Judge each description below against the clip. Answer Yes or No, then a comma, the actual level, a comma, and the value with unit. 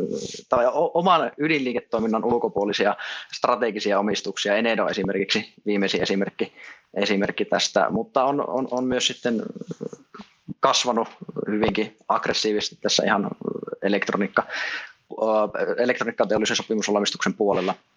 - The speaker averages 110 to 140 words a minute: No, slow, 95 wpm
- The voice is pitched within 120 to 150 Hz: No, low, 110 Hz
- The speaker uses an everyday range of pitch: Yes, average, 3.1 semitones